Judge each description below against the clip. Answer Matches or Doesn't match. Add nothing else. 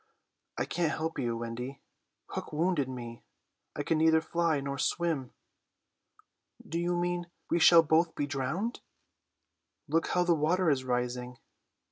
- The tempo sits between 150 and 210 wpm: Doesn't match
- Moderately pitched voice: Matches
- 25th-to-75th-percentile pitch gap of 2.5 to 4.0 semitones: Doesn't match